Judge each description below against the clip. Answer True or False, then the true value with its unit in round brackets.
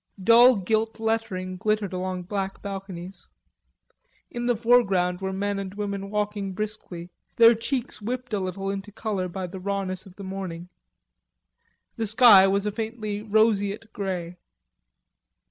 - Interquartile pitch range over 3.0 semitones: False (2.6 semitones)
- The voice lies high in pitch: True (200 Hz)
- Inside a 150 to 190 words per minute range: False (140 wpm)